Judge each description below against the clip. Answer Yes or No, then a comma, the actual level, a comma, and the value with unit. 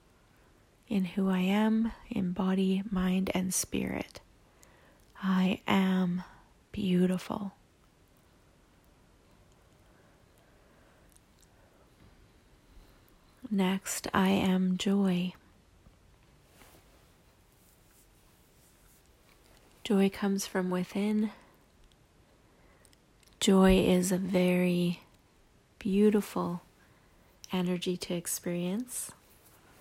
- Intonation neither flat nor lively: No, narrow, 1.6 semitones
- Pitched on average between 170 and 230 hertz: Yes, high, 190 Hz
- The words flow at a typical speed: No, slow, 55 wpm